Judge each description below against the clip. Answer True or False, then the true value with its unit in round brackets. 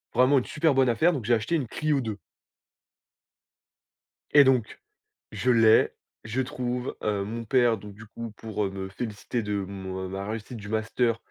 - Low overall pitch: True (115 Hz)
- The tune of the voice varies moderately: True (3.4 semitones)